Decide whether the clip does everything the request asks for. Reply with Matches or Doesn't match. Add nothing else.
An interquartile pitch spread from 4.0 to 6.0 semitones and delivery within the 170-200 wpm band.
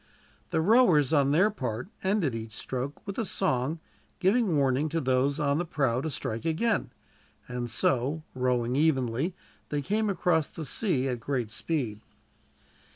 Doesn't match